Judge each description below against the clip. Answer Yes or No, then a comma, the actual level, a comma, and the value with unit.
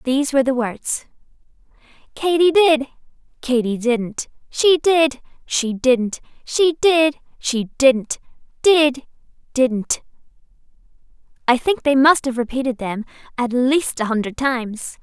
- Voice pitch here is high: Yes, very high, 265 Hz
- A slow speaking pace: Yes, slow, 115 wpm